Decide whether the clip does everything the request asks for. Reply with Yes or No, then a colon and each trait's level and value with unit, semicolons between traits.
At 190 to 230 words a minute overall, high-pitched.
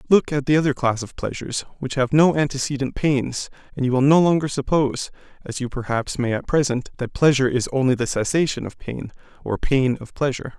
No: fast, 205 wpm; low, 135 Hz